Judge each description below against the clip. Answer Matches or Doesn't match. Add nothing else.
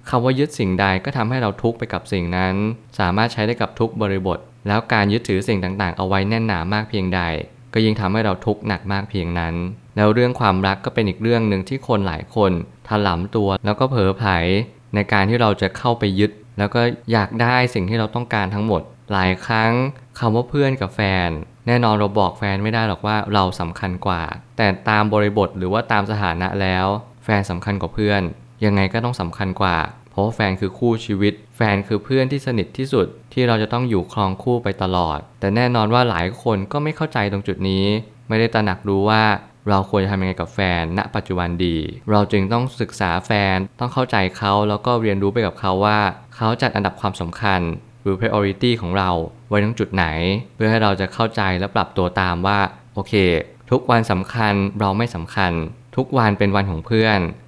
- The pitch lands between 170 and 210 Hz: Doesn't match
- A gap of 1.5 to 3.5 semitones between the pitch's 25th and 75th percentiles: Matches